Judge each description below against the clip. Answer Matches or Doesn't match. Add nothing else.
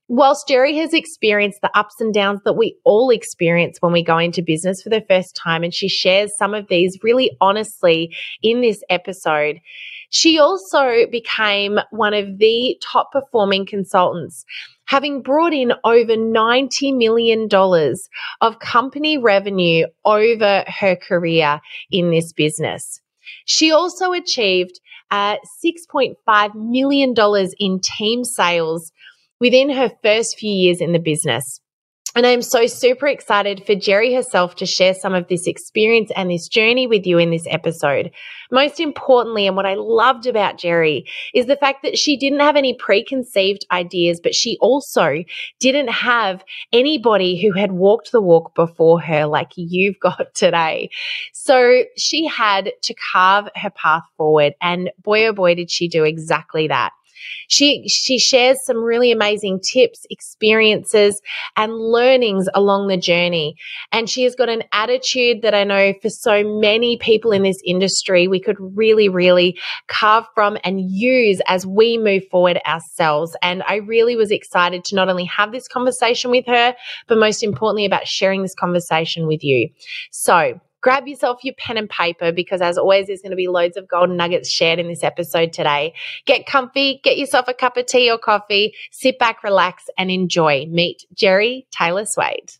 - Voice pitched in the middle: Doesn't match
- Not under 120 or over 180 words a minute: Matches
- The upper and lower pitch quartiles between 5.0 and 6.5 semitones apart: Matches